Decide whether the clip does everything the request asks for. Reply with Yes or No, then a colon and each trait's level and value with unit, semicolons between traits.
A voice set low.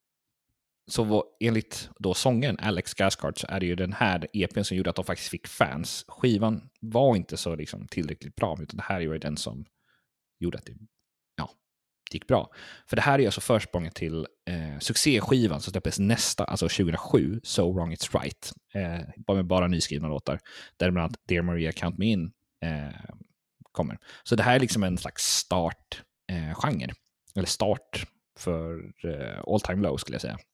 Yes: very low, 95 Hz